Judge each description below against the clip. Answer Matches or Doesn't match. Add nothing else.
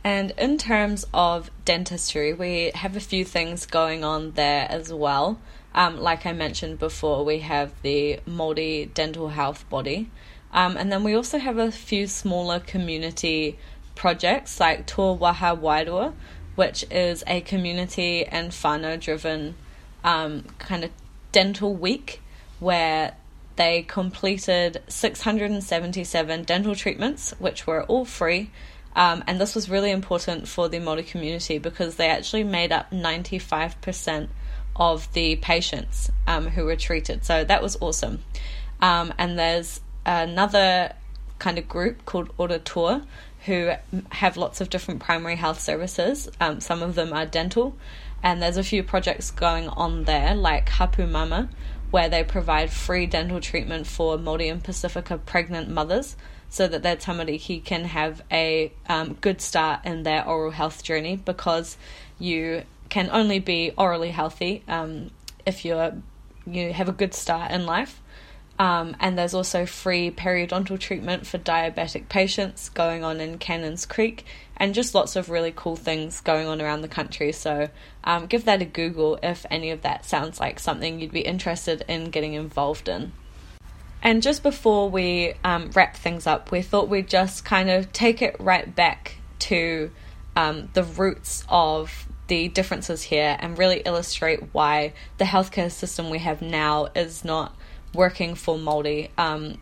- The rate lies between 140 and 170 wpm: Matches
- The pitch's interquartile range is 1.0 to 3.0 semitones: Matches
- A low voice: Doesn't match